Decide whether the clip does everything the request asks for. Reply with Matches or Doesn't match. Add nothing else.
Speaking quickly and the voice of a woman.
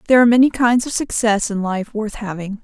Matches